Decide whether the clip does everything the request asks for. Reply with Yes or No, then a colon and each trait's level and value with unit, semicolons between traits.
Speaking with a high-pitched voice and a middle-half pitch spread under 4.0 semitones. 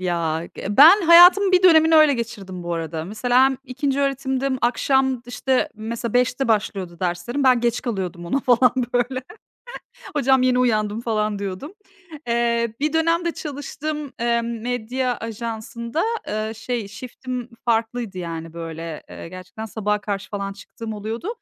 No: high, 235 Hz; average, 4.5 semitones